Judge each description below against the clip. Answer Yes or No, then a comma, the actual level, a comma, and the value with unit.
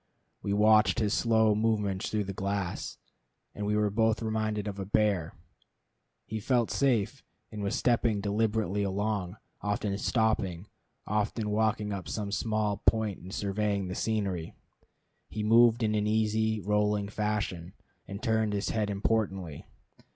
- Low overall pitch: Yes, low, 105 Hz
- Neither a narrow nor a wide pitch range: No, narrow, 1.6 semitones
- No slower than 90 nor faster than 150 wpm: Yes, average, 140 wpm